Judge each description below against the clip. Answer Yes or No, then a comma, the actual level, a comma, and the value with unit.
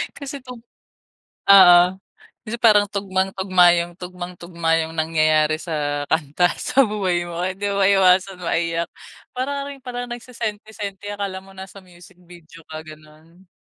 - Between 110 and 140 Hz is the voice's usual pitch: No, medium, 185 Hz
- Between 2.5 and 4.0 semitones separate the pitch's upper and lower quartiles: Yes, average, 3.4 semitones